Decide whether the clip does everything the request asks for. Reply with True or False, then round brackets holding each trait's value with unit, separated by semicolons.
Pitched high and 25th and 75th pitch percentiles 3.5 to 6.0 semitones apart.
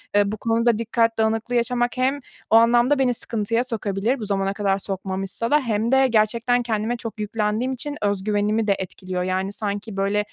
False (220 Hz; 2.9 semitones)